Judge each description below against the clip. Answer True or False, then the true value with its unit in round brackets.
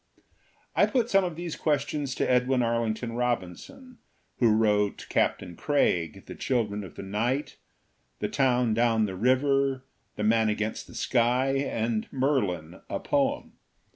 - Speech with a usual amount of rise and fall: True (4.3 semitones)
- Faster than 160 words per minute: False (150 wpm)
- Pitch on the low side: True (120 Hz)